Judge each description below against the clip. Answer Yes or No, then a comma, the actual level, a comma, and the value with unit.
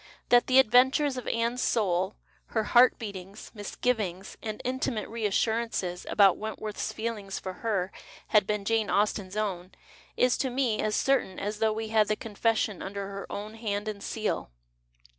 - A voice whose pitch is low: No, high, 215 Hz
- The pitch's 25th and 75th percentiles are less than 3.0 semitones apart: Yes, narrow, 2.5 semitones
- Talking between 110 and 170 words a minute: Yes, average, 160 wpm